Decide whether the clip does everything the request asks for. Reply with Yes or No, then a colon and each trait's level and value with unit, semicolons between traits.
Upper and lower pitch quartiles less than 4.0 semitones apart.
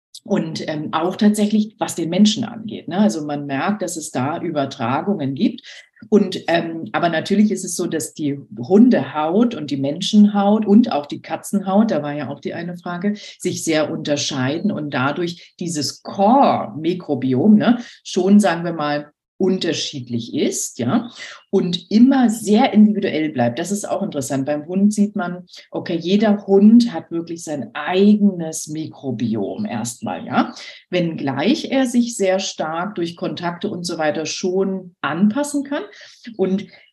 No: average, 5.1 semitones